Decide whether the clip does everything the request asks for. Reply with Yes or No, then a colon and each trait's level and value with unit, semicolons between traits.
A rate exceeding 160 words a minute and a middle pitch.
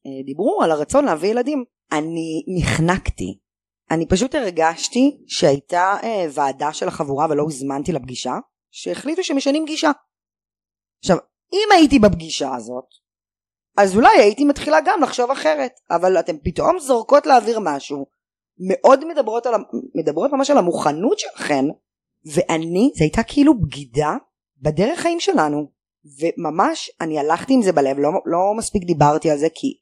No: slow, 135 wpm; medium, 180 Hz